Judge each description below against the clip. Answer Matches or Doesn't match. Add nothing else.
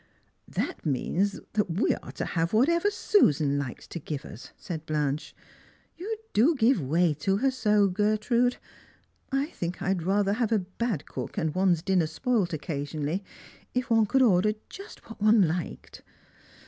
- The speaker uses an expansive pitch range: Matches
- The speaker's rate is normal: Matches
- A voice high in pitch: Matches